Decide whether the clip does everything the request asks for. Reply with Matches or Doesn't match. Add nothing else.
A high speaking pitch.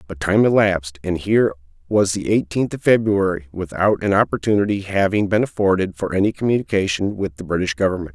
Doesn't match